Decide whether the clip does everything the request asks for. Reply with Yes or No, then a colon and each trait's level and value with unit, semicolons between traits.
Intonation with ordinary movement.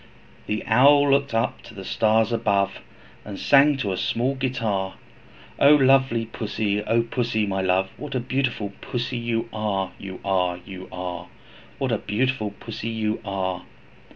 Yes: average, 4.5 semitones